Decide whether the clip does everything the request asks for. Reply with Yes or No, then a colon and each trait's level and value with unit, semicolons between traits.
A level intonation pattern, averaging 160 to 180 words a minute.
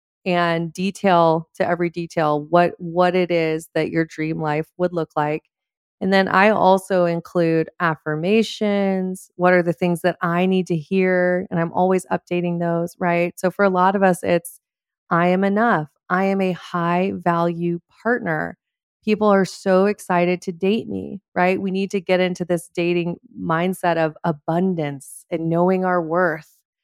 Yes: narrow, 1.9 semitones; average, 170 wpm